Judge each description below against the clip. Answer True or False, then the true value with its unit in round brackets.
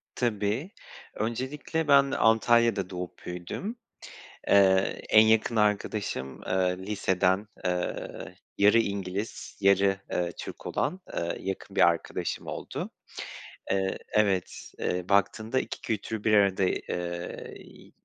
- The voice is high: False (100 Hz)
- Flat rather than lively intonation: False (3.2 semitones)